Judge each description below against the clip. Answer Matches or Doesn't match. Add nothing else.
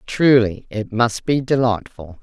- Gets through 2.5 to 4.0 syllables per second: Matches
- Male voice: Doesn't match